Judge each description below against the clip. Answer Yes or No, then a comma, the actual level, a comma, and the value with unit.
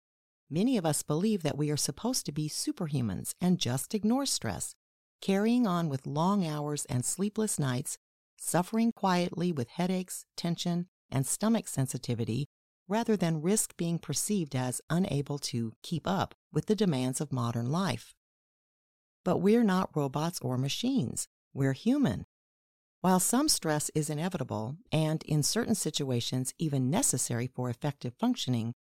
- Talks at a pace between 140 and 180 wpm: Yes, average, 145 wpm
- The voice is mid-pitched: Yes, medium, 155 Hz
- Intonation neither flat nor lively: No, wide, 6.7 semitones